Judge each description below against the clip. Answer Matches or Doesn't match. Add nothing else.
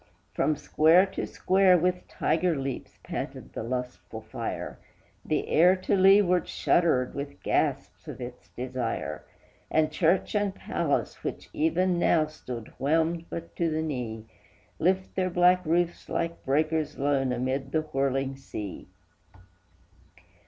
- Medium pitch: Matches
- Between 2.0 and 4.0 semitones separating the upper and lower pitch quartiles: Doesn't match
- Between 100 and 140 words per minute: Matches